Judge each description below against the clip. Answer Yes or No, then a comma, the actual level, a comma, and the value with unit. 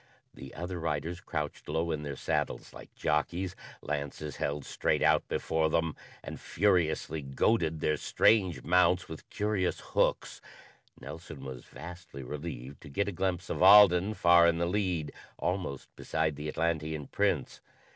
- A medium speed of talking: Yes, average, 145 wpm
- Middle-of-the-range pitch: No, very low, 80 Hz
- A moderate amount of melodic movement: Yes, average, 3.3 semitones